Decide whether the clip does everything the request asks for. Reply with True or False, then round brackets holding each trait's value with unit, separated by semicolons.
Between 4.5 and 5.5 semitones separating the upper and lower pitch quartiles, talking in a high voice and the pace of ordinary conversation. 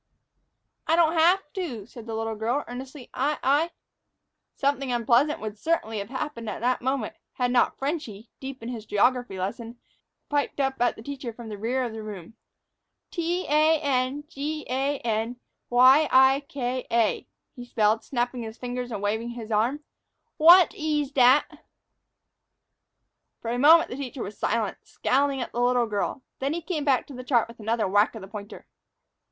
False (4.0 semitones; 250 Hz; 180 wpm)